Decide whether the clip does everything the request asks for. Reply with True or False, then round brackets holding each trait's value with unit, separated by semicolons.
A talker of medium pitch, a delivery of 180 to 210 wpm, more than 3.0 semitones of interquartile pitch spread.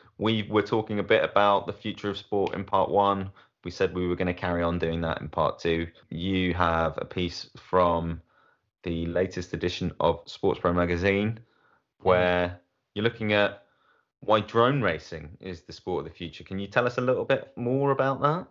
False (95 Hz; 200 wpm; 3.7 semitones)